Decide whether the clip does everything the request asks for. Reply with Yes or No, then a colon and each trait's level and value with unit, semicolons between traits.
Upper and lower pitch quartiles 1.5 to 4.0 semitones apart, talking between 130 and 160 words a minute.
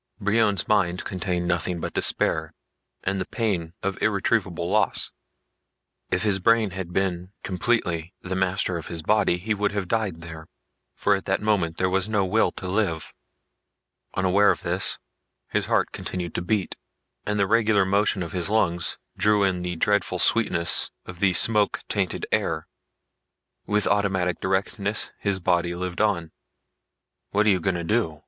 Yes: average, 2.8 semitones; average, 155 wpm